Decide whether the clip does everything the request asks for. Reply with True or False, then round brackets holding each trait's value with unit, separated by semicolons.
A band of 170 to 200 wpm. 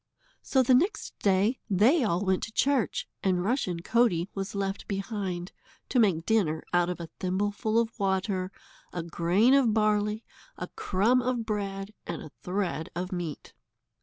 False (160 wpm)